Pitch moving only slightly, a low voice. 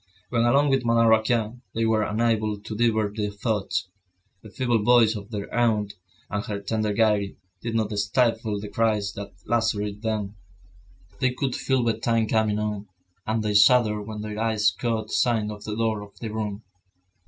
Yes: narrow, 1.7 semitones; low, 110 Hz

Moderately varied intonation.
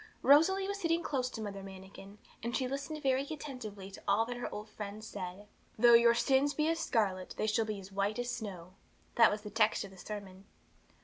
Yes: average, 4.9 semitones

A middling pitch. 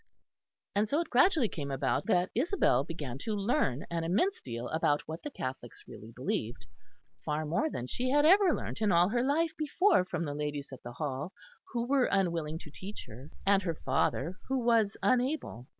Yes: medium, 180 Hz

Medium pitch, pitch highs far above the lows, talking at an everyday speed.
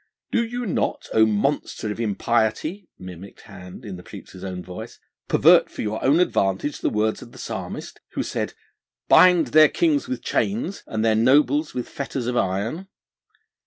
No: low, 120 Hz; wide, 7.7 semitones; average, 165 wpm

